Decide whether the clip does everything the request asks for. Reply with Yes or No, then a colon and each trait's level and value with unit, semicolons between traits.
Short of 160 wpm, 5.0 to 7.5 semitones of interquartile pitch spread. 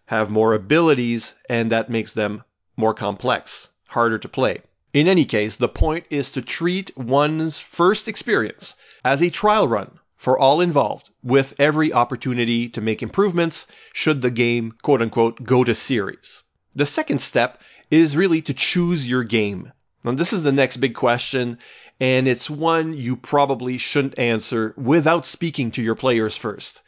No: average, 165 wpm; average, 5.3 semitones